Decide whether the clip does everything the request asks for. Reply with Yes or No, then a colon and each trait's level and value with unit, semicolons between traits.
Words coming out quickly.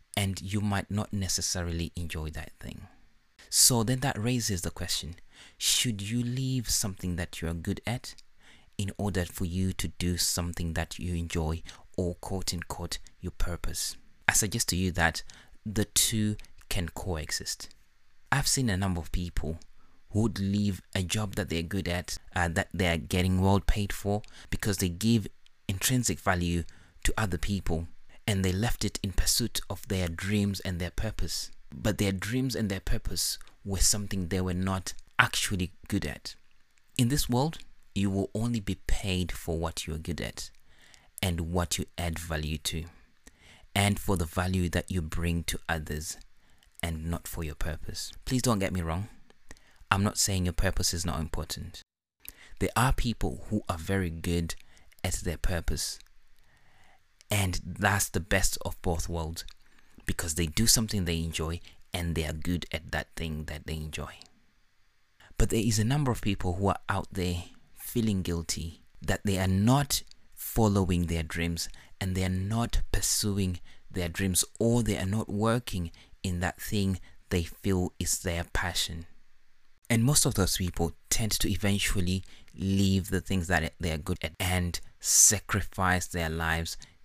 No: average, 170 wpm